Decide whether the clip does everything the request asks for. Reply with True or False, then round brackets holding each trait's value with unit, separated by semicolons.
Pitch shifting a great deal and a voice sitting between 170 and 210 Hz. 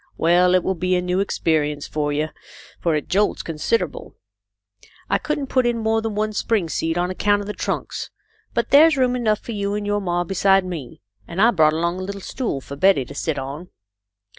False (4.6 semitones; 185 Hz)